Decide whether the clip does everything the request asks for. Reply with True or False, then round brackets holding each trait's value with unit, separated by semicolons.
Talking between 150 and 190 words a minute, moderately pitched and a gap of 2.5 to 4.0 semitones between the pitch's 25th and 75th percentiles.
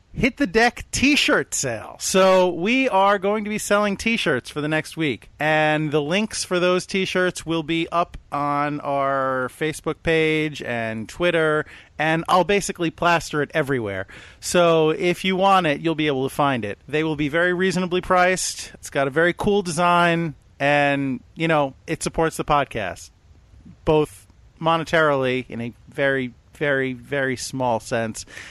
False (170 wpm; 155 Hz; 4.8 semitones)